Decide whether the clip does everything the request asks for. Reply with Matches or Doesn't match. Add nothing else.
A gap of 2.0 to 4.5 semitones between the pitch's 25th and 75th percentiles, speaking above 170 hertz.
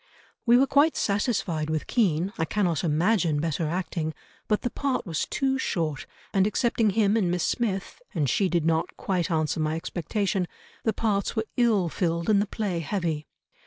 Doesn't match